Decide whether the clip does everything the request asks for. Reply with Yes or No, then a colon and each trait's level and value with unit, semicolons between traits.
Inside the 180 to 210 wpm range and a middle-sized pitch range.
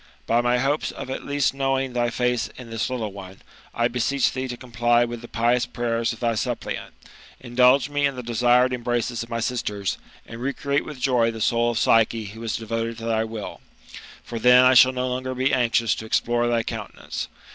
No: fast, 205 wpm; narrow, 1.7 semitones